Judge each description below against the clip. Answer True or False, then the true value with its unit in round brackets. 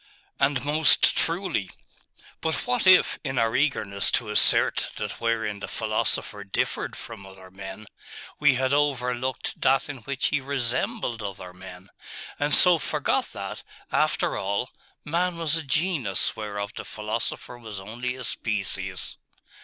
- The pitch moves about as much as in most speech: False (6.2 semitones)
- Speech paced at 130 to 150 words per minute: True (140 wpm)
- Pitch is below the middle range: True (120 Hz)